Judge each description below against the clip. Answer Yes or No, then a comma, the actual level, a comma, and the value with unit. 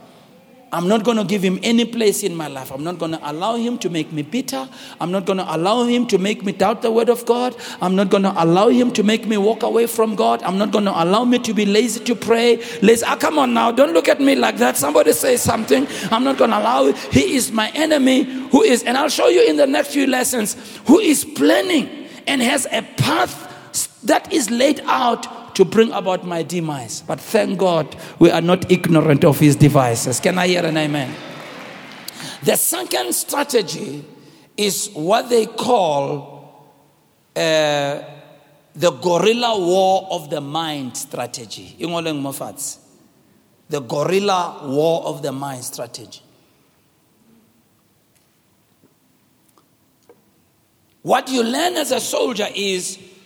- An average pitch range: No, wide, 6.5 semitones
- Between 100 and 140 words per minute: No, average, 165 wpm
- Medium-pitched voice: No, high, 210 Hz